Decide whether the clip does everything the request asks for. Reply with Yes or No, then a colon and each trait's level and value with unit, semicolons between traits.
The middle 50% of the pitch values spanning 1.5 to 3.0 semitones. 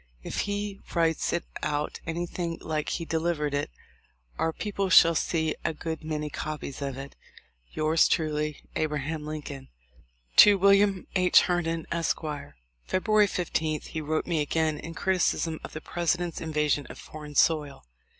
Yes: narrow, 2.4 semitones